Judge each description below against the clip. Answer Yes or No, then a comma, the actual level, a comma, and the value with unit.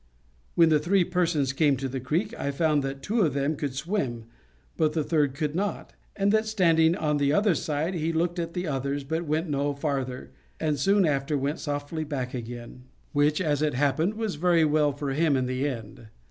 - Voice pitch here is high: No, medium, 150 Hz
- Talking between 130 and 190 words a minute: No, fast, 205 wpm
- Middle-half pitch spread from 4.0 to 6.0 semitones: No, average, 3.3 semitones